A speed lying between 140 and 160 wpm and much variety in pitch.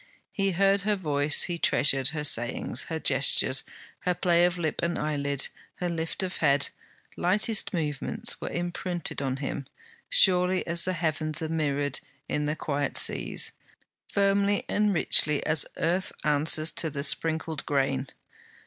No: average, 150 wpm; average, 3.9 semitones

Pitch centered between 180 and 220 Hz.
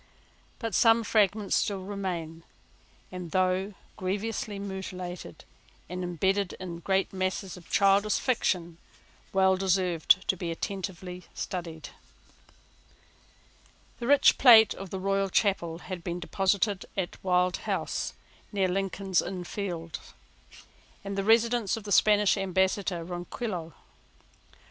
Yes: high, 190 Hz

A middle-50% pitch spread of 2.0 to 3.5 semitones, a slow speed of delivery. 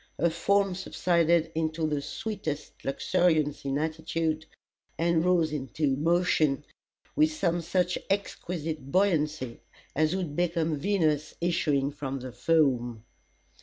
Yes: average, 2.9 semitones; slow, 115 wpm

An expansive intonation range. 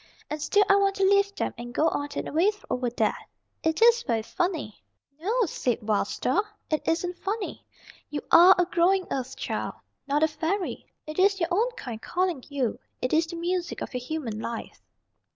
Yes: wide, 6.6 semitones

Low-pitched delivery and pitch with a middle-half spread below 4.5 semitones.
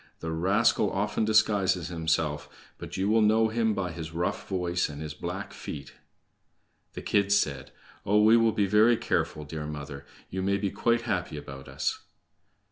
No: very low, 95 Hz; average, 5.2 semitones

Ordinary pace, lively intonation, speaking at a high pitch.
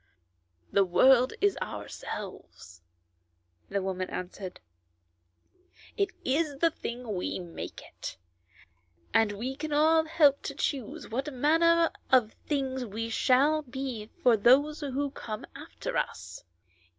No: slow, 125 wpm; wide, 5.9 semitones; very high, 260 Hz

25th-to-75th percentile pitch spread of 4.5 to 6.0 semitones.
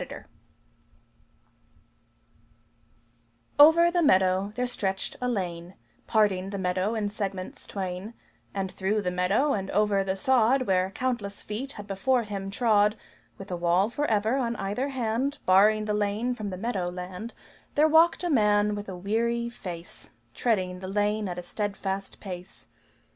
No: average, 3.7 semitones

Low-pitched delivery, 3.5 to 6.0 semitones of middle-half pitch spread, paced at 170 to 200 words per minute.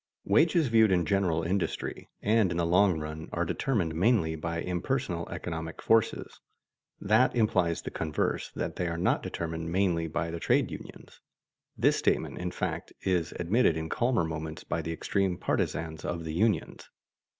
No: very low, 85 Hz; average, 3.8 semitones; average, 160 wpm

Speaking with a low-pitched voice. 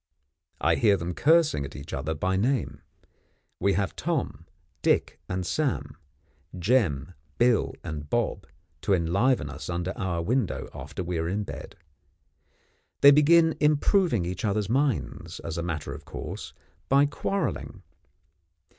Yes: very low, 95 Hz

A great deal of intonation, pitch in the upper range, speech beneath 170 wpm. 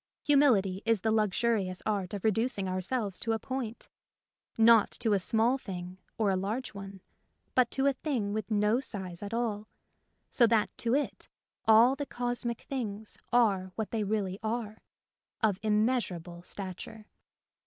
No: average, 3.3 semitones; high, 220 Hz; average, 160 wpm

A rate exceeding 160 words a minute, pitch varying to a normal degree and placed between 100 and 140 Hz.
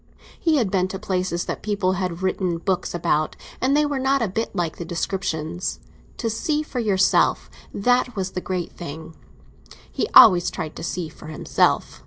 No: average, 175 wpm; average, 4.7 semitones; medium, 185 Hz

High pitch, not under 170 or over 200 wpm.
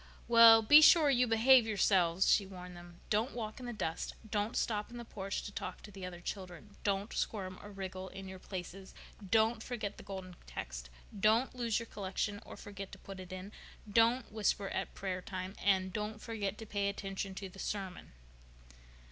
Yes: high, 200 Hz; average, 190 wpm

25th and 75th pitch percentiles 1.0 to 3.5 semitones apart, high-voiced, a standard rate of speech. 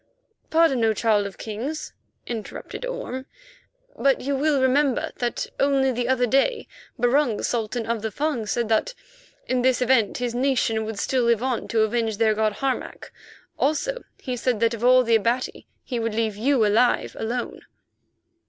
Yes: average, 3.0 semitones; high, 245 Hz; average, 165 wpm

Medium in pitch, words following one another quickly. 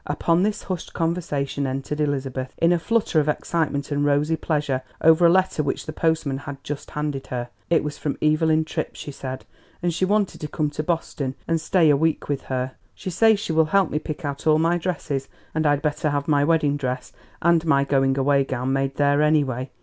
Yes: medium, 150 Hz; fast, 215 wpm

